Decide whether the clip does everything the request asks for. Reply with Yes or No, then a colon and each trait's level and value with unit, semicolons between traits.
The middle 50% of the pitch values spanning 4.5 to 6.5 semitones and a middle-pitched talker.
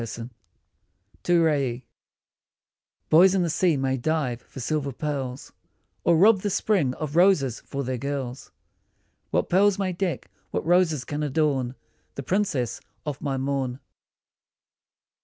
Yes: average, 4.9 semitones; medium, 145 Hz